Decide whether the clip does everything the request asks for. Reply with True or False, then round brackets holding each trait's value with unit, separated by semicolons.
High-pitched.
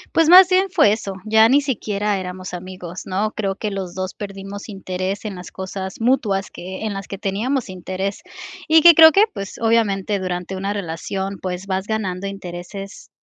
True (195 Hz)